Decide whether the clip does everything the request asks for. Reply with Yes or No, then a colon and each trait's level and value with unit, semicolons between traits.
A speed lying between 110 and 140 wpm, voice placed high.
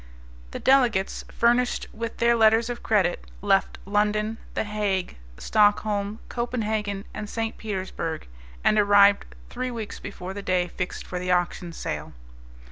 Yes: slow, 135 wpm; high, 210 Hz